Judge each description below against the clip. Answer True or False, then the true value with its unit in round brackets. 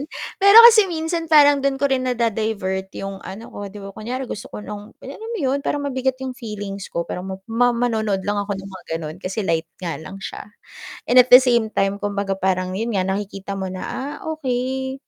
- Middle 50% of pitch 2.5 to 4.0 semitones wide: False (5.3 semitones)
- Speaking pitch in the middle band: False (215 Hz)